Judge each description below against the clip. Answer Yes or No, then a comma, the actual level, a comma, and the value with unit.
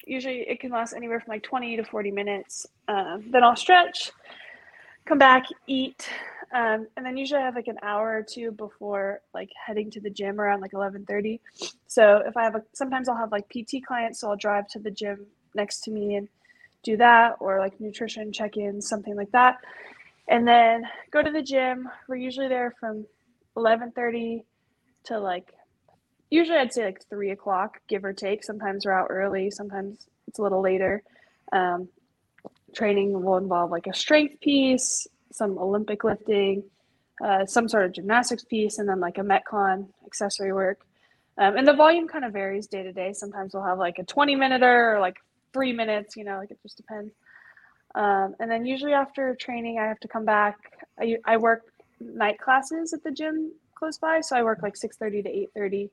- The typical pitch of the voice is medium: No, high, 220 Hz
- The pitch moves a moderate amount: Yes, average, 3.9 semitones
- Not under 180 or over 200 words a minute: Yes, average, 195 wpm